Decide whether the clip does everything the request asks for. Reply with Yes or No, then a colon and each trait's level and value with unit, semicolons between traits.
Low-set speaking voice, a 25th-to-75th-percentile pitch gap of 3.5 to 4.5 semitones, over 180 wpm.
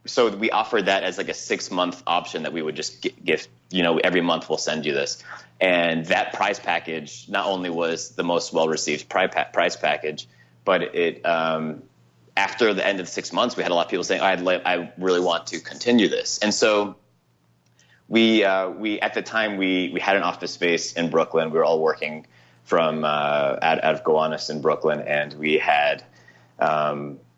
Yes: very low, 80 Hz; average, 3.9 semitones; fast, 205 wpm